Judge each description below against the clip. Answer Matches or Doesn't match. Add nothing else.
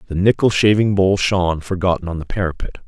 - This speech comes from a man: Matches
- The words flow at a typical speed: Matches